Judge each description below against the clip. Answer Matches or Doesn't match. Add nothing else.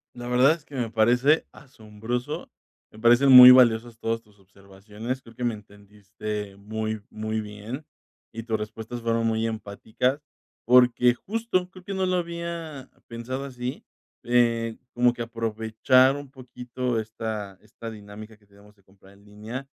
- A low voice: Matches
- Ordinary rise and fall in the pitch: Matches